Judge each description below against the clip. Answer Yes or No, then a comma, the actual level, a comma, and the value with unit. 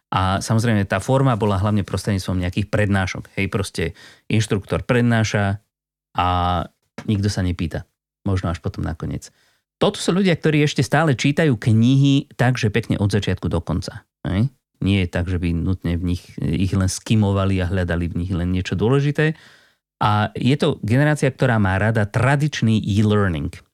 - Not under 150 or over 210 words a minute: Yes, average, 160 wpm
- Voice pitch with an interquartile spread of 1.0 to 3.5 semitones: No, average, 4.6 semitones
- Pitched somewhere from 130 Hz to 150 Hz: No, low, 105 Hz